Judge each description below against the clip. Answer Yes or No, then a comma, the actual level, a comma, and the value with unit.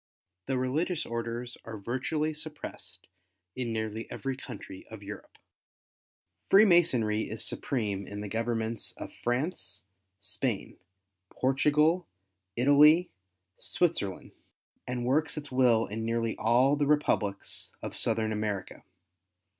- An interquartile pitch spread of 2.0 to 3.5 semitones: No, average, 5.1 semitones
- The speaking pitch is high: No, low, 120 Hz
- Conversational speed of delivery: No, slow, 110 wpm